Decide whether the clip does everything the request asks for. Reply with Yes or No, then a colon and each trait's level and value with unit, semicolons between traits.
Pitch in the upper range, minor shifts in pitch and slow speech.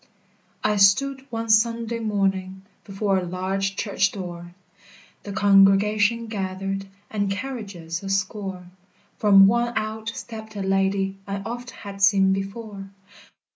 Yes: high, 200 Hz; narrow, 2.1 semitones; slow, 125 wpm